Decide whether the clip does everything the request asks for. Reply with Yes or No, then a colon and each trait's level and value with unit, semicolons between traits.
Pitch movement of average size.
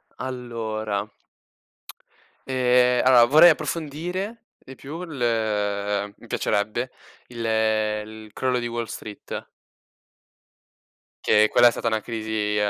Yes: average, 3.4 semitones